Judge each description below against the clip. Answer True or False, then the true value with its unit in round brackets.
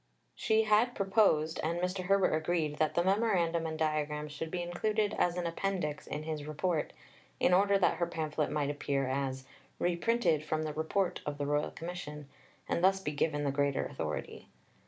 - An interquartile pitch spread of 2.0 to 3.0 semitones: False (3.7 semitones)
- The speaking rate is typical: True (175 wpm)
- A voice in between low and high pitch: True (160 Hz)